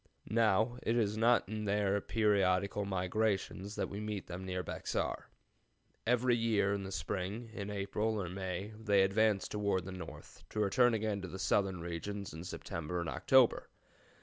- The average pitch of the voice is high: No, low, 100 Hz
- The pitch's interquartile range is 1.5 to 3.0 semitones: Yes, narrow, 2.5 semitones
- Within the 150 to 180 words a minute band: Yes, average, 165 wpm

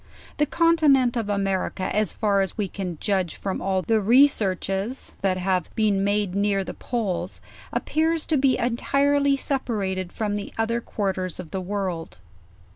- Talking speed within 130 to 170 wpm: Yes, average, 160 wpm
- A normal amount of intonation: Yes, average, 4.5 semitones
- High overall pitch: Yes, high, 205 Hz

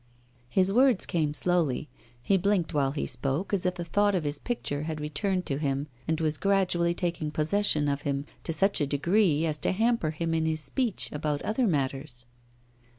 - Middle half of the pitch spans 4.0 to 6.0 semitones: Yes, average, 4.6 semitones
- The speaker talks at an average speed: Yes, average, 190 wpm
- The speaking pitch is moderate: Yes, medium, 160 Hz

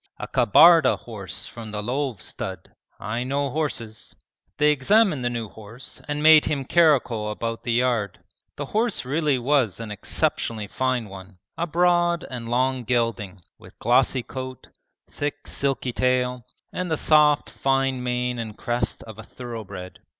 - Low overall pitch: Yes, low, 125 Hz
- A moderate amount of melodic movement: Yes, average, 4.2 semitones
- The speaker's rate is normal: Yes, average, 150 wpm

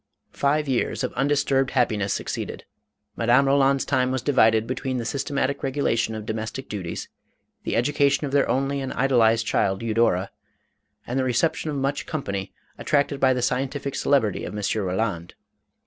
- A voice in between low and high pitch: No, low, 130 Hz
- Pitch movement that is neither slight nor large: Yes, average, 3.7 semitones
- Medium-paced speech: Yes, average, 160 wpm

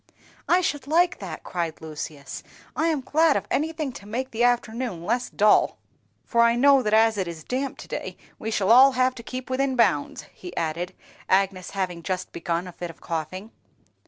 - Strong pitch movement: Yes, wide, 6.5 semitones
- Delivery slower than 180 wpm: No, average, 190 wpm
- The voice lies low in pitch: No, high, 220 Hz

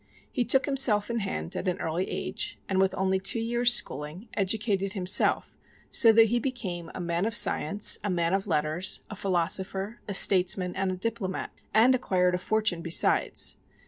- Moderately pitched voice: No, high, 195 Hz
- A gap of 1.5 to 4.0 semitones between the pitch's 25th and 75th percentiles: Yes, average, 3.6 semitones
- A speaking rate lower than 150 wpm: No, average, 175 wpm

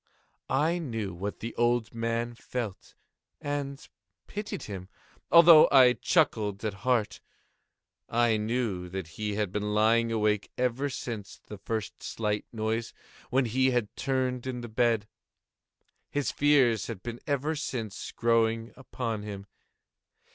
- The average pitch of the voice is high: No, low, 115 Hz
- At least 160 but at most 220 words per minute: No, slow, 135 wpm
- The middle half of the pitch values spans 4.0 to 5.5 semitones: No, average, 3.3 semitones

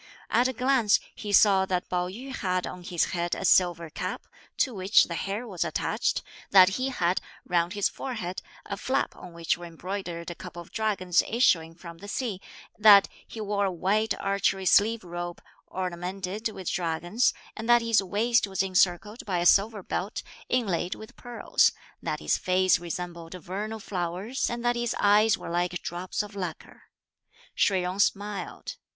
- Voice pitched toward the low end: No, high, 190 Hz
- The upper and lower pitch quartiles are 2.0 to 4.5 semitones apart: Yes, average, 3.5 semitones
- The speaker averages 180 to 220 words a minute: No, average, 170 wpm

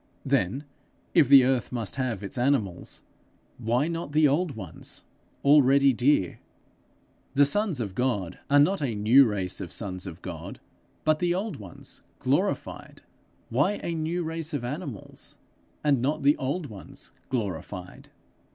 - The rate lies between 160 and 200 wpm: No, average, 145 wpm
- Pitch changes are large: Yes, wide, 6.3 semitones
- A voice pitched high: No, low, 135 Hz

